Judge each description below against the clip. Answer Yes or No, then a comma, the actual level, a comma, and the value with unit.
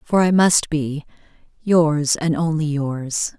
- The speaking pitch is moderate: Yes, medium, 155 Hz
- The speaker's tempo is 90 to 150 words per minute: Yes, average, 140 wpm